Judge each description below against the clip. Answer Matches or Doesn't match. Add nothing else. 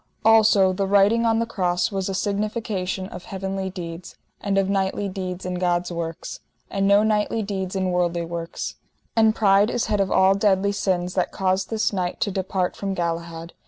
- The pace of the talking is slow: Doesn't match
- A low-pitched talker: Doesn't match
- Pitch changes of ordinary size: Doesn't match